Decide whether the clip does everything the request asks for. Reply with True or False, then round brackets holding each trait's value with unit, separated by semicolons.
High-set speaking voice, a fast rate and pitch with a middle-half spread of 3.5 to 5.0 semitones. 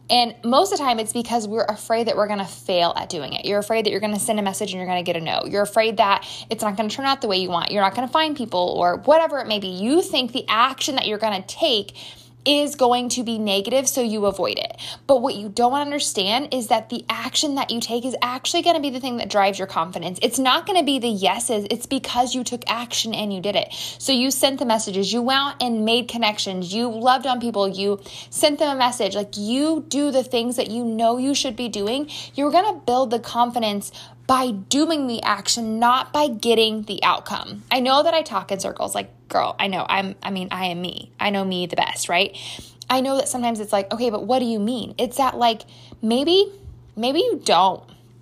True (235 Hz; 245 wpm; 4.2 semitones)